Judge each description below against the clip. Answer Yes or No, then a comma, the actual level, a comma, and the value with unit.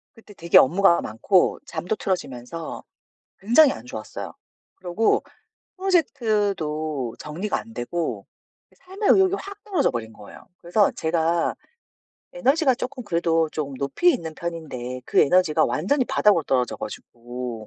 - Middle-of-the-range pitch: Yes, medium, 170 Hz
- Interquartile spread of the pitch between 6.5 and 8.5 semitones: Yes, wide, 7.6 semitones